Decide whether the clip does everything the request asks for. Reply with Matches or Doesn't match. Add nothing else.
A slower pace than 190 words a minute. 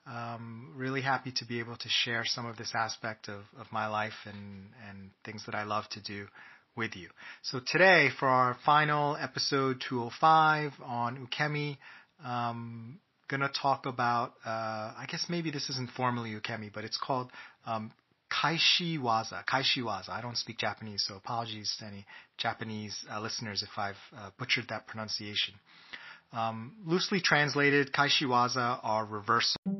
Matches